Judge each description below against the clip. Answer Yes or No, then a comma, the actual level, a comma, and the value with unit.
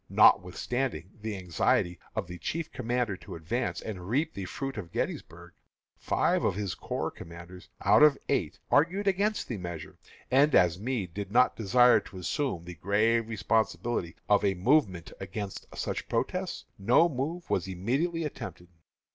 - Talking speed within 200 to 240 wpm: No, average, 155 wpm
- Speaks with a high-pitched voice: No, low, 110 Hz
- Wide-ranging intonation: Yes, wide, 6.7 semitones